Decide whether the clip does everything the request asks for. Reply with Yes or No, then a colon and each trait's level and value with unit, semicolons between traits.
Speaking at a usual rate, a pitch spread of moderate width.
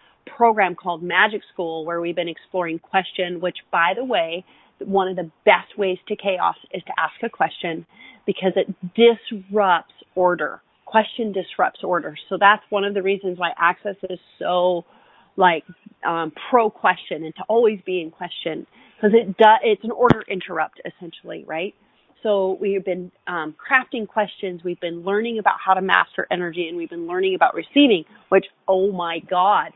Yes: average, 170 wpm; average, 3.5 semitones